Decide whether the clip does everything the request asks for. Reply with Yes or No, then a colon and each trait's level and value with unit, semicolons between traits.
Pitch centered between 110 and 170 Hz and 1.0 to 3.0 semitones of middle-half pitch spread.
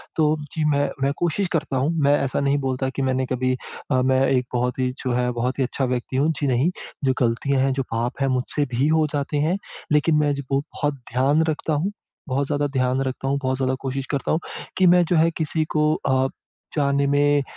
Yes: medium, 140 Hz; narrow, 2.4 semitones